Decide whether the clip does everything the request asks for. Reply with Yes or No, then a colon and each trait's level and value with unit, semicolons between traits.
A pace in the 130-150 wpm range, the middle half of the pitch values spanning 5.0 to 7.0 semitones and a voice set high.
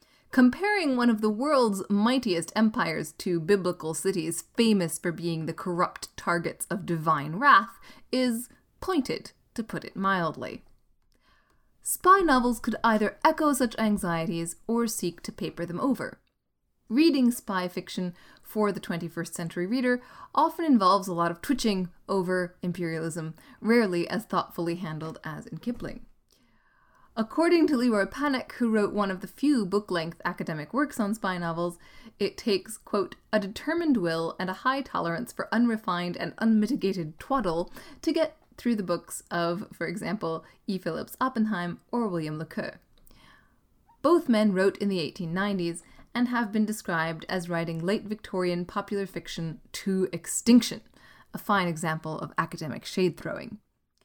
Yes: average, 145 wpm; wide, 5.5 semitones; high, 200 Hz